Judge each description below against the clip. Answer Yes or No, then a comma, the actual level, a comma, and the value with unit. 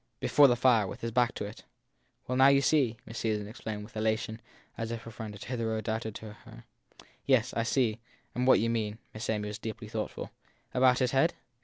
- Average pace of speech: No, fast, 210 wpm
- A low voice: Yes, low, 115 Hz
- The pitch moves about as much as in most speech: No, narrow, 2.3 semitones